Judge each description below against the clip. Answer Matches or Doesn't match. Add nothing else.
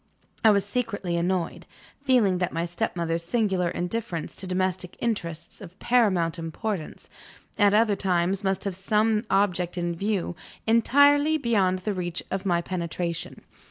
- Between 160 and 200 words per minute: Doesn't match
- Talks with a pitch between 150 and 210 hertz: Matches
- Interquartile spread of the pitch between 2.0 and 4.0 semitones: Matches